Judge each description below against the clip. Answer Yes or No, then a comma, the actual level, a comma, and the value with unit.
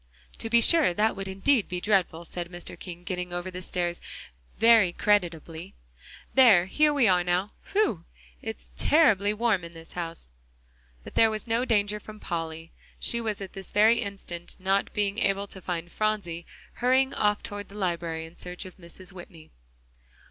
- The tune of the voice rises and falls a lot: No, average, 3.6 semitones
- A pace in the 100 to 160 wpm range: No, average, 170 wpm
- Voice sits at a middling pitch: No, high, 195 Hz